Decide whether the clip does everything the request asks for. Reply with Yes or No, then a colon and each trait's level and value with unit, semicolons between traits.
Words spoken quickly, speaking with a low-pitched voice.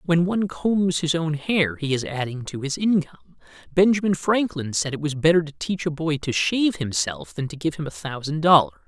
No: fast, 215 wpm; medium, 155 Hz